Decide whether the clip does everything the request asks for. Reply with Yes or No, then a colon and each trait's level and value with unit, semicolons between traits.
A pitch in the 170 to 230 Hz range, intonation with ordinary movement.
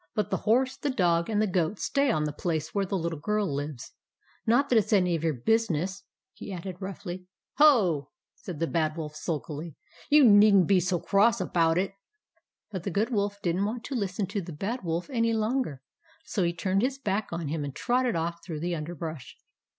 Yes: medium, 185 Hz; average, 4.6 semitones